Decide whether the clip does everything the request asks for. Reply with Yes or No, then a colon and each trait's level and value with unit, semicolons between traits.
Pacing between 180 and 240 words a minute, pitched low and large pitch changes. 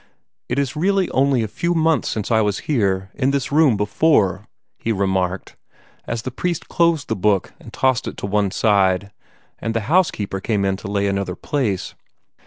Yes: average, 185 wpm; low, 110 Hz; wide, 6.2 semitones